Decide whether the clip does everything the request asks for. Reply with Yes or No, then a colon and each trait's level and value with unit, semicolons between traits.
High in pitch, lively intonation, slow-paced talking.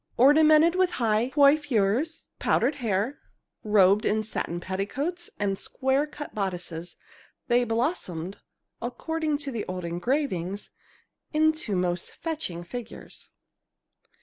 Yes: high, 235 Hz; wide, 7.5 semitones; slow, 105 wpm